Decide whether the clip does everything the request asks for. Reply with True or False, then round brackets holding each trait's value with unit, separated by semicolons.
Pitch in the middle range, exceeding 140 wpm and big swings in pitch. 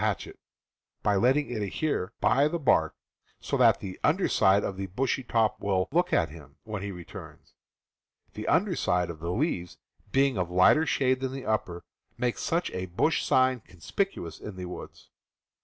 False (105 Hz; 190 wpm; 6.8 semitones)